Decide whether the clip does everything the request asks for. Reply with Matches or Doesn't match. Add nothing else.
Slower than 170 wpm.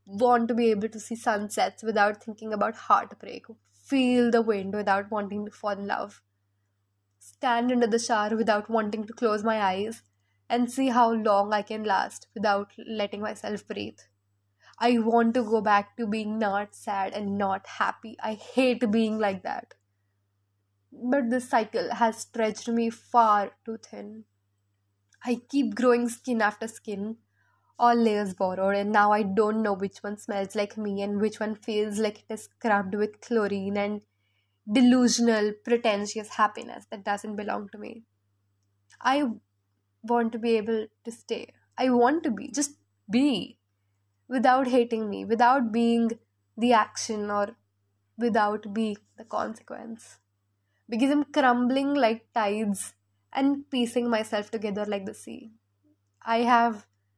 Matches